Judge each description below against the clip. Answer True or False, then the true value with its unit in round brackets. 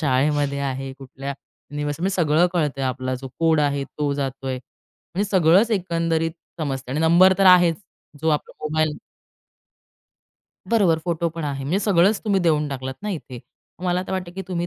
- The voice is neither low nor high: True (160 Hz)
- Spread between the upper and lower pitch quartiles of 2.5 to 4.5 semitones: True (4.1 semitones)